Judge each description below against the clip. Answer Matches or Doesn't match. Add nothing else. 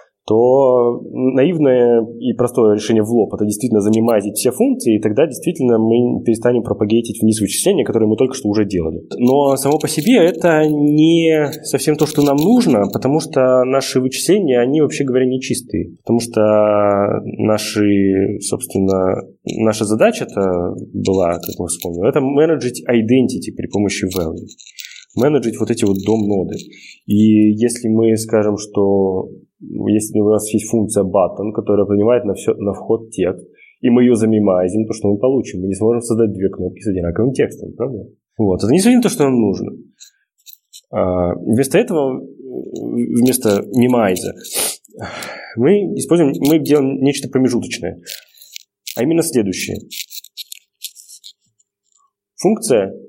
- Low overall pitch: Matches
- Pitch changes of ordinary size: Matches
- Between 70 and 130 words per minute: Doesn't match